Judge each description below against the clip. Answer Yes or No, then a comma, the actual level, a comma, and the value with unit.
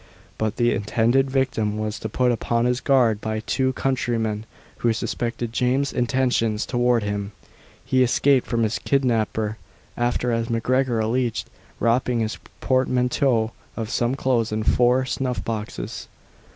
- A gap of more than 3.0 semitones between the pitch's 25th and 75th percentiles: No, narrow, 2.5 semitones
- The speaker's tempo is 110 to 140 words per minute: Yes, slow, 135 wpm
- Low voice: Yes, low, 120 Hz